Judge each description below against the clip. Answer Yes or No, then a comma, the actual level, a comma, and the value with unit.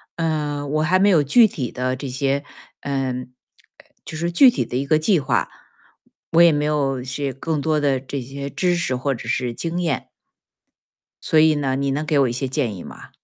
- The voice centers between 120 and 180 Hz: Yes, medium, 140 Hz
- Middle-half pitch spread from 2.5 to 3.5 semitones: Yes, average, 3.1 semitones